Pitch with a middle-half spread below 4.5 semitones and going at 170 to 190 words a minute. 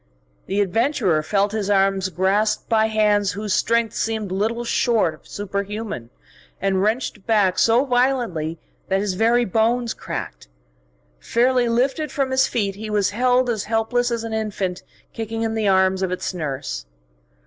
No: average, 3.3 semitones; average, 155 wpm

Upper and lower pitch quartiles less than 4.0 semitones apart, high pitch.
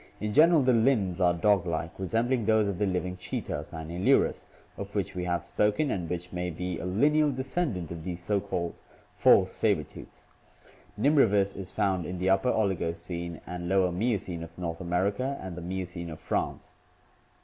No: average, 3.3 semitones; very low, 95 Hz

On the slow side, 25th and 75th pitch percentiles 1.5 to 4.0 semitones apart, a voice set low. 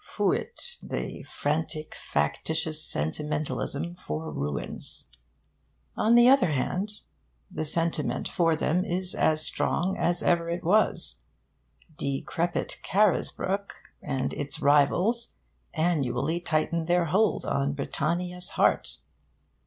No: slow, 105 wpm; average, 3.5 semitones; medium, 165 Hz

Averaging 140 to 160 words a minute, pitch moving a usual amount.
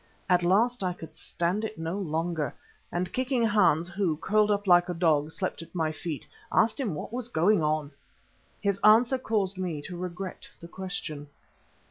No: average, 175 wpm; average, 4.2 semitones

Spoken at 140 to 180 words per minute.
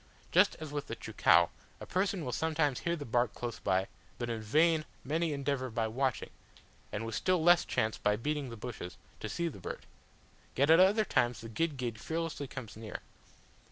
No: average, 195 wpm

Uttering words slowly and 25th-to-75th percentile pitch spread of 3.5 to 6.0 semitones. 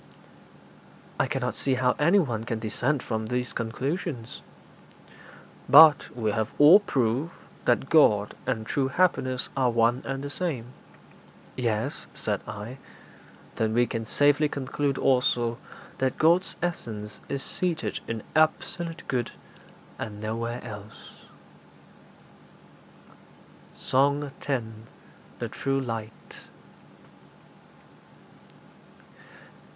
Yes: slow, 100 wpm; average, 4.2 semitones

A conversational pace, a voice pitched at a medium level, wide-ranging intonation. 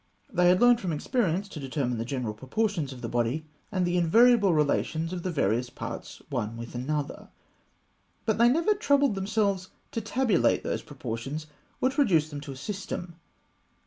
Yes: average, 175 wpm; medium, 170 Hz; wide, 7.6 semitones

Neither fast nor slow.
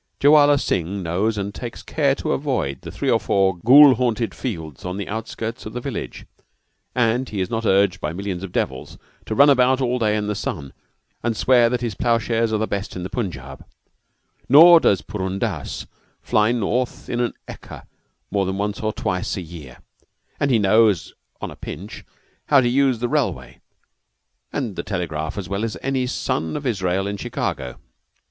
Yes: average, 185 wpm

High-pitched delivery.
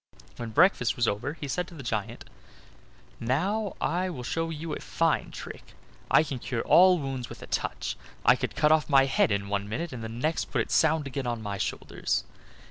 No: low, 135 Hz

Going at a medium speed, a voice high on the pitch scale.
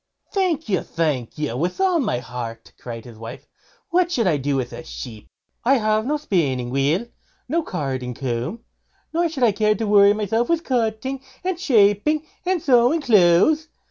Yes: average, 175 wpm; high, 210 Hz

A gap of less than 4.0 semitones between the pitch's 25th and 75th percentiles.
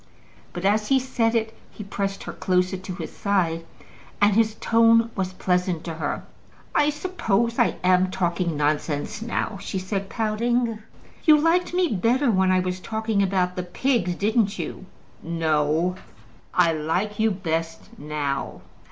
No: average, 4.3 semitones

